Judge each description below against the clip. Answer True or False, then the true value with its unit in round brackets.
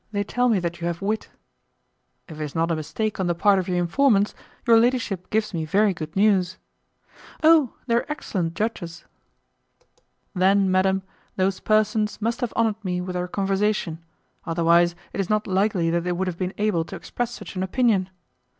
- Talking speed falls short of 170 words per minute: False (185 wpm)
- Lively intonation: False (3.7 semitones)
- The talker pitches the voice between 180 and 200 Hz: True (190 Hz)